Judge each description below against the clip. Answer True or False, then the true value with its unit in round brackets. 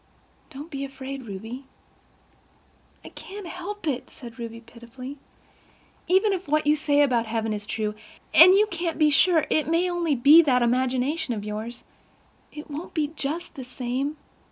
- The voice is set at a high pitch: True (275 Hz)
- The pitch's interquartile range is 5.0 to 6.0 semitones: True (5.3 semitones)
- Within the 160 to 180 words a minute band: False (150 wpm)